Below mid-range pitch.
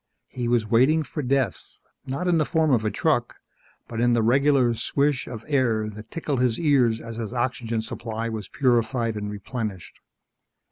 Yes: low, 120 Hz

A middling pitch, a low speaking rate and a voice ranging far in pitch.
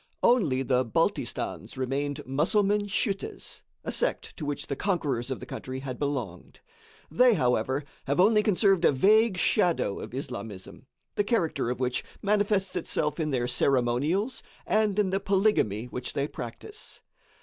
No: medium, 150 Hz; average, 150 wpm; wide, 7.7 semitones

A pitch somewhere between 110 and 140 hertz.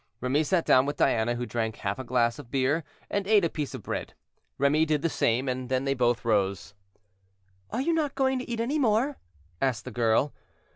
Yes: low, 135 Hz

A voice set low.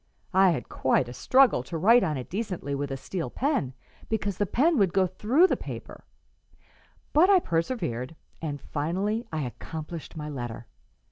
No: medium, 175 Hz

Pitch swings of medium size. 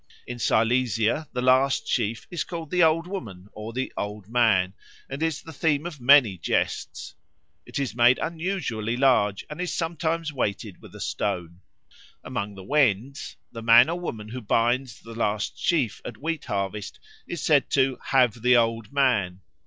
No: wide, 5.8 semitones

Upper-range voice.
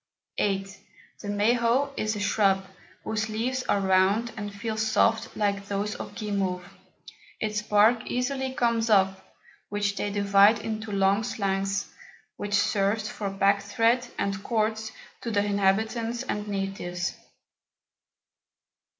Yes: high, 205 Hz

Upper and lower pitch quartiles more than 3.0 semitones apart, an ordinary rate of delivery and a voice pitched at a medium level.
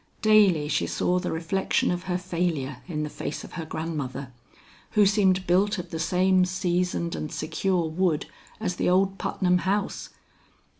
No: average, 2.7 semitones; average, 160 wpm; medium, 180 Hz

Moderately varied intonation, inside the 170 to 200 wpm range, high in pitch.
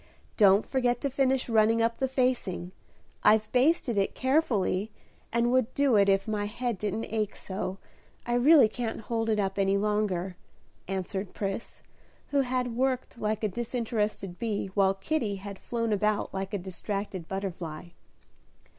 No: average, 3.8 semitones; average, 155 wpm; high, 215 Hz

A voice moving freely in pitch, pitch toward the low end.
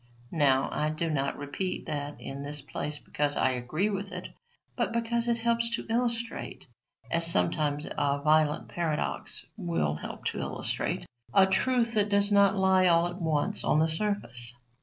No: wide, 5.8 semitones; medium, 165 Hz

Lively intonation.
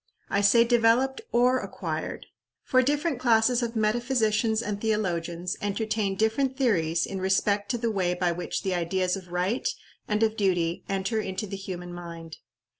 No: average, 4.2 semitones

